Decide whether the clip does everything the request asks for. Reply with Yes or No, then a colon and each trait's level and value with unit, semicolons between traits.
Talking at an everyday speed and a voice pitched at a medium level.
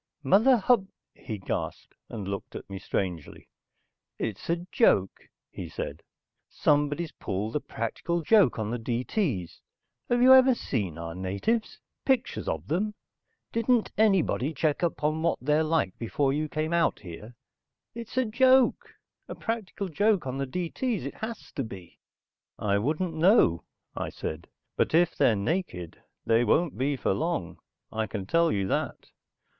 Yes: average, 155 wpm; medium, 150 Hz